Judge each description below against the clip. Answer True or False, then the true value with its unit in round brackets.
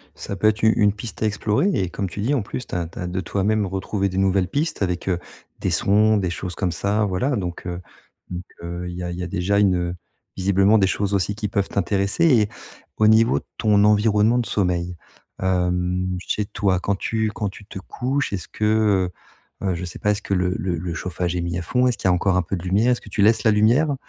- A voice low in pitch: True (100 Hz)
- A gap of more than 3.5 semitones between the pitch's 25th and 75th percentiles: False (2.9 semitones)